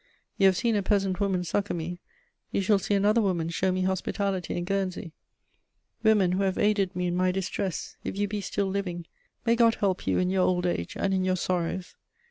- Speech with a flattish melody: Yes, narrow, 1.8 semitones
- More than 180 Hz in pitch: Yes, high, 190 Hz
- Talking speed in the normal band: No, fast, 210 wpm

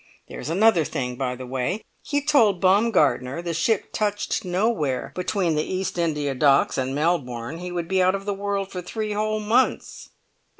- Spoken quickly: No, average, 175 wpm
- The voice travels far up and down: Yes, wide, 6.0 semitones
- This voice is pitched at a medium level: Yes, medium, 180 Hz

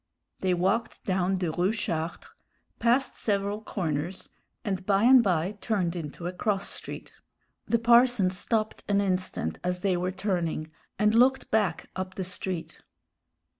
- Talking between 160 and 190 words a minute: No, average, 145 wpm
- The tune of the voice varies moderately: Yes, average, 3.1 semitones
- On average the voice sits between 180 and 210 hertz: Yes, high, 190 Hz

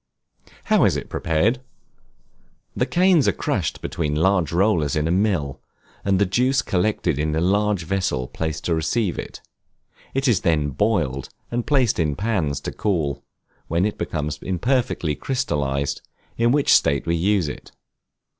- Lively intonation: Yes, wide, 6.1 semitones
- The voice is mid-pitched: No, very low, 90 Hz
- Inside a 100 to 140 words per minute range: No, average, 155 wpm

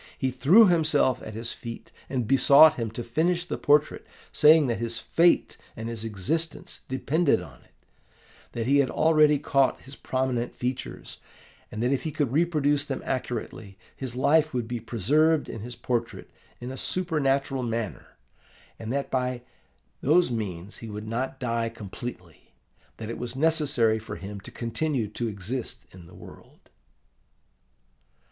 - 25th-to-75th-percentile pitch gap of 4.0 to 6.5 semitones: Yes, average, 4.3 semitones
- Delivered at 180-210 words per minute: No, average, 155 wpm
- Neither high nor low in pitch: No, low, 125 Hz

